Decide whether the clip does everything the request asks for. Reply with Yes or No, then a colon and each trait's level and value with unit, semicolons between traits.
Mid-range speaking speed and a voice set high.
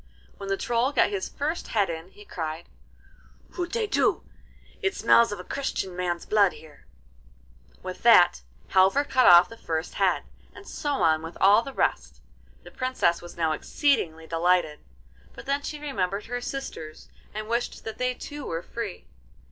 Yes: average, 165 wpm; high, 200 Hz